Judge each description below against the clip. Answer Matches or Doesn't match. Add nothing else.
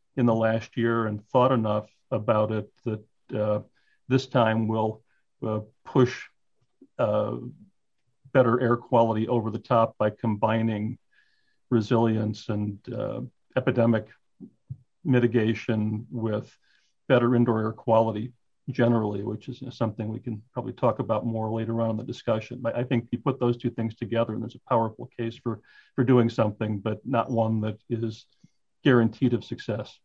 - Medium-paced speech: Matches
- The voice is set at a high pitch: Doesn't match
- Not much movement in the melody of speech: Matches